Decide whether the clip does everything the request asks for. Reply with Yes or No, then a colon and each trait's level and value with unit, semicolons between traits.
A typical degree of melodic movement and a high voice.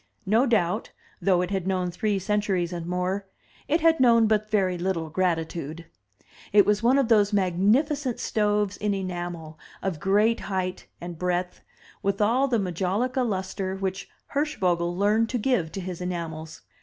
Yes: average, 3.3 semitones; high, 195 Hz